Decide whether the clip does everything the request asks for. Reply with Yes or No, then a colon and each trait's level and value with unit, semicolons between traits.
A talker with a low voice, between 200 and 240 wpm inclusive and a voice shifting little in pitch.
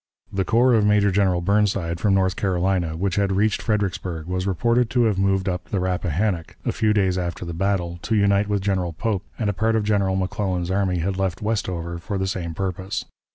Yes: very low, 95 Hz; fast, 205 wpm; narrow, 2.3 semitones